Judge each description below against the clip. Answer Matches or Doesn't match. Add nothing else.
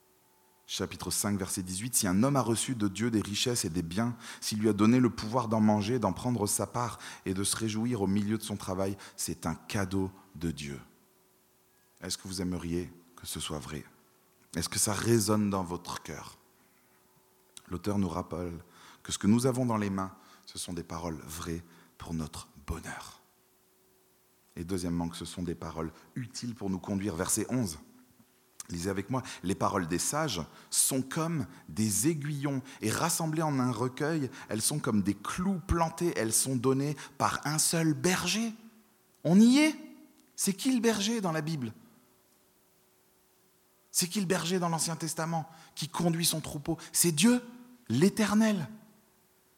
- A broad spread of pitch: Matches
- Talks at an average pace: Matches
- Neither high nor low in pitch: Doesn't match